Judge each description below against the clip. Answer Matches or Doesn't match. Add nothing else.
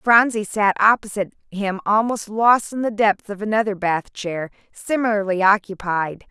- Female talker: Matches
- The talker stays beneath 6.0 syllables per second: Matches